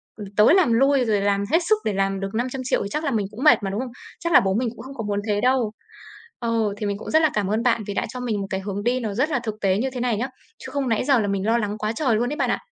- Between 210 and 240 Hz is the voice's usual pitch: Yes, high, 225 Hz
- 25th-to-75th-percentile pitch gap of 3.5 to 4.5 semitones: Yes, average, 3.9 semitones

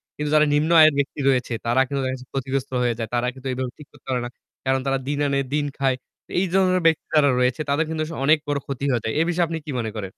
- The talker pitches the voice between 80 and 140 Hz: Yes, low, 135 Hz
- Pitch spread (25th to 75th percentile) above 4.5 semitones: No, average, 3.3 semitones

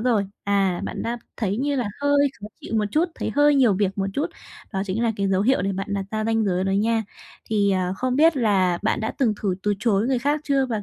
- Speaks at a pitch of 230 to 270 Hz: No, high, 215 Hz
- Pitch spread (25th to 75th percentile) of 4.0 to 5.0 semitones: Yes, average, 4.6 semitones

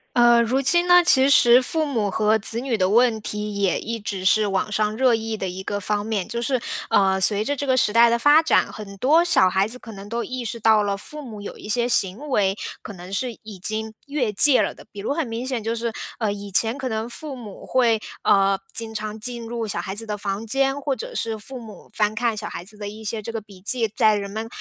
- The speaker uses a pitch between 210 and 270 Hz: Yes, high, 220 Hz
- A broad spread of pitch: No, average, 3.3 semitones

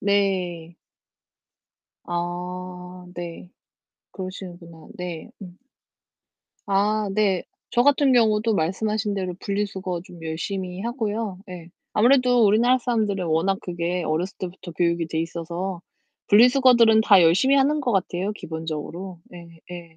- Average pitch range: Yes, average, 3.6 semitones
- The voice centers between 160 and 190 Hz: Yes, medium, 185 Hz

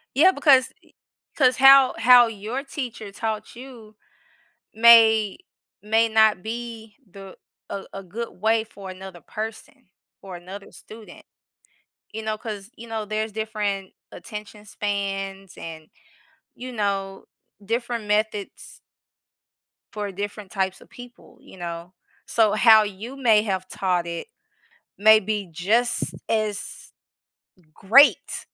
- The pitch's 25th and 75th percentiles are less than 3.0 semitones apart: Yes, narrow, 2.6 semitones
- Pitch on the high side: Yes, high, 215 Hz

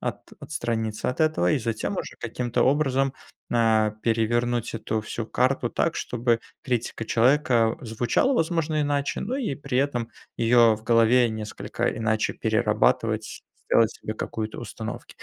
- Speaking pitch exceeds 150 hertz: No, low, 120 Hz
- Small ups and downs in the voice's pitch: No, average, 3.5 semitones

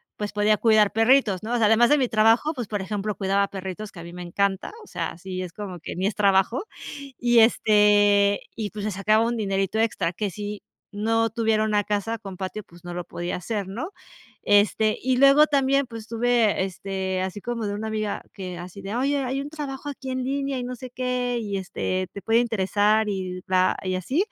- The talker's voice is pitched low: No, high, 210 Hz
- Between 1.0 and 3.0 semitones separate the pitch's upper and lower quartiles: No, average, 3.7 semitones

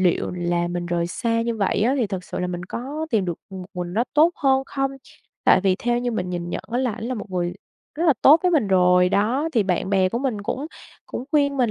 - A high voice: Yes, high, 210 Hz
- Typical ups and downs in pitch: No, wide, 6.3 semitones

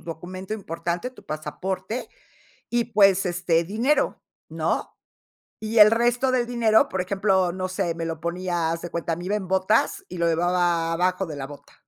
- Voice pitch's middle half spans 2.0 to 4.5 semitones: Yes, average, 3.9 semitones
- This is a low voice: No, medium, 185 Hz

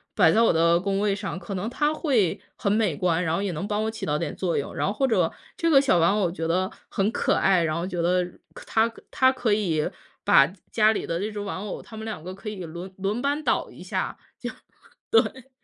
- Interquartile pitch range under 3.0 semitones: No, average, 4.3 semitones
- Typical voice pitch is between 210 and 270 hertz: No, high, 195 Hz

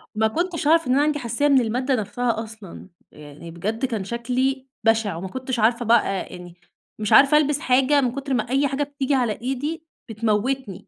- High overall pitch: Yes, very high, 250 Hz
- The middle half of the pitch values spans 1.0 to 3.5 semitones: No, average, 3.9 semitones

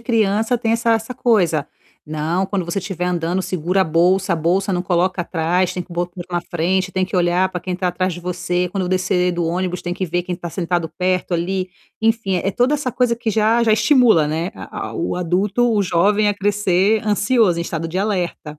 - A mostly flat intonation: No, average, 3.0 semitones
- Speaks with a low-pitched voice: No, medium, 185 Hz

